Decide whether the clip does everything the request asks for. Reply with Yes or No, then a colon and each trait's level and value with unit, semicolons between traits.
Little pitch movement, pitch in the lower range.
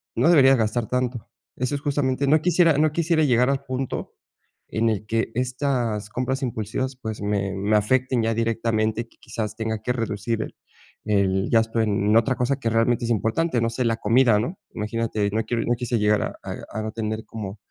No: average, 3.0 semitones; low, 115 Hz